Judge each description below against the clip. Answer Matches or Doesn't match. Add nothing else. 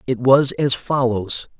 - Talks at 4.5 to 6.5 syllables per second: Doesn't match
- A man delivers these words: Matches